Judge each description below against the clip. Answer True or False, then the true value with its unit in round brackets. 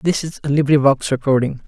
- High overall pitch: False (140 Hz)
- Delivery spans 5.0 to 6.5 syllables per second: True (6.1 syllables/s)